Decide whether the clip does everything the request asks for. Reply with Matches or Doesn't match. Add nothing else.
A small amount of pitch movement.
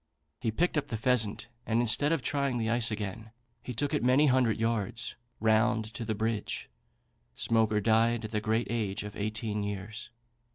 Matches